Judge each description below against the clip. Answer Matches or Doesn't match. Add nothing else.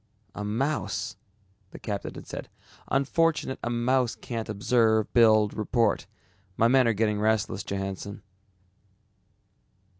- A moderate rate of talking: Doesn't match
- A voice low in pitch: Matches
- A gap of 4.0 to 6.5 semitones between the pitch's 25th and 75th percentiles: Doesn't match